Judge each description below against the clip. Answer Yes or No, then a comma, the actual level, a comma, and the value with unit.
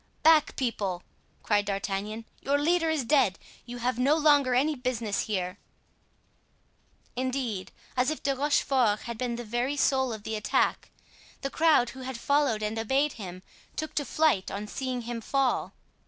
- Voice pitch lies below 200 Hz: No, very high, 250 Hz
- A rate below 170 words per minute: Yes, average, 160 wpm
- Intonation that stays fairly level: No, average, 4.6 semitones